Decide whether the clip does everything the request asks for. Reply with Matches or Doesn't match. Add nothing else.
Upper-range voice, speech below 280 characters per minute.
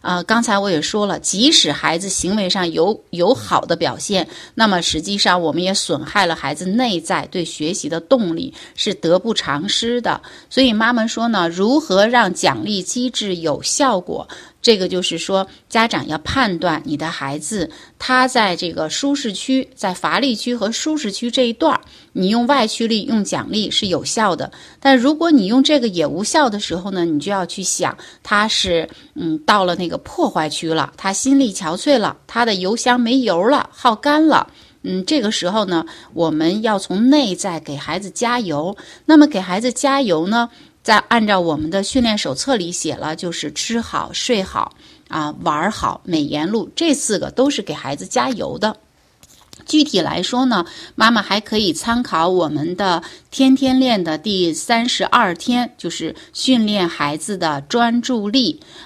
Matches